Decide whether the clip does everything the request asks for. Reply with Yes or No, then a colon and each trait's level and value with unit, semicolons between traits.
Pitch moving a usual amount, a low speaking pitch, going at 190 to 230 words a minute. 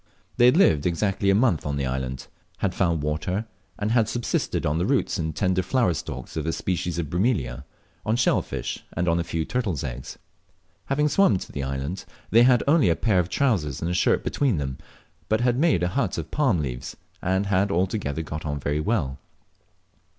No: wide, 6.7 semitones; very low, 90 Hz; average, 200 wpm